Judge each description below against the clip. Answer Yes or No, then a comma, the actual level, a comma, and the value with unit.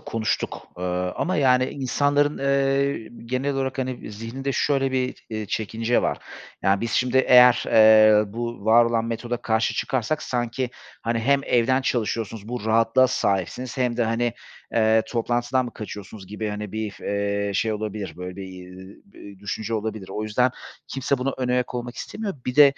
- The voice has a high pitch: No, low, 115 Hz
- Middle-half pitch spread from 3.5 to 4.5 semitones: No, average, 3.1 semitones